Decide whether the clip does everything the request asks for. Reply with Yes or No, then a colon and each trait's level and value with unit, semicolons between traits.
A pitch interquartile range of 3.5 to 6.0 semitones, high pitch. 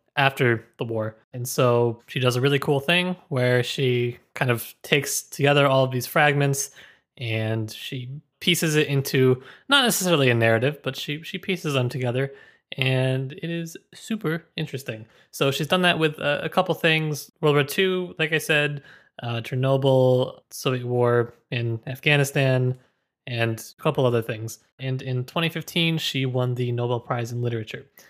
No: average, 3.8 semitones; low, 135 Hz